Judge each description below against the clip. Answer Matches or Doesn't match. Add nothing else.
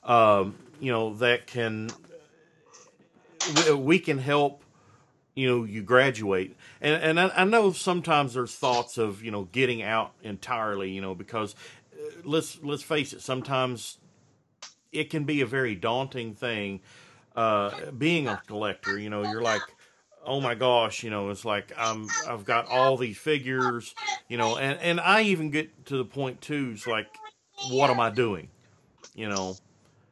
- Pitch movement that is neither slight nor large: Matches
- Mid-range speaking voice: Doesn't match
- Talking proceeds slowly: Doesn't match